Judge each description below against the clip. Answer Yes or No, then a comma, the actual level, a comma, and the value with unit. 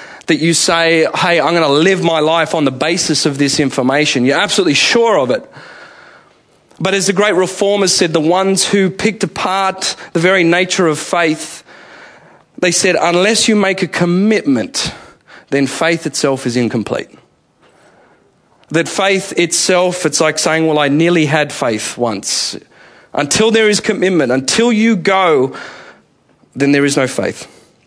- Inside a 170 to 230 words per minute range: No, average, 155 wpm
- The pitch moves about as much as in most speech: Yes, average, 3.8 semitones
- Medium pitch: Yes, medium, 175 Hz